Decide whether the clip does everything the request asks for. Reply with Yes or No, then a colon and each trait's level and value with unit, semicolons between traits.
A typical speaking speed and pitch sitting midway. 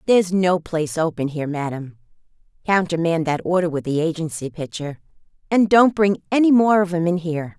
Yes: average, 175 wpm; medium, 170 Hz